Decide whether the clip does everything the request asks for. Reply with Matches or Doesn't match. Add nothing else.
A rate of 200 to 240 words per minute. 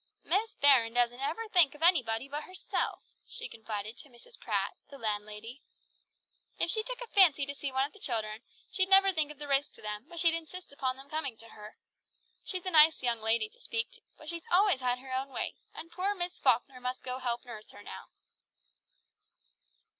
Matches